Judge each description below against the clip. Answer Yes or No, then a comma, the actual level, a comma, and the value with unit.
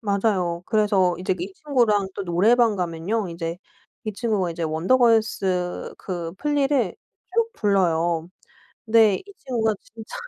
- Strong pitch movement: No, average, 4.5 semitones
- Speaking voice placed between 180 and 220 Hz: Yes, high, 200 Hz